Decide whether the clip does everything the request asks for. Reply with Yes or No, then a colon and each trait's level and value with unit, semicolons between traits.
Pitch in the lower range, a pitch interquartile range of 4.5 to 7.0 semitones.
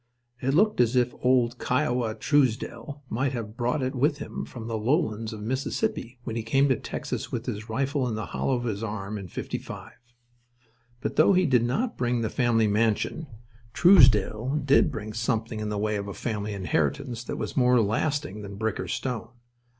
No: low, 120 Hz; average, 3.5 semitones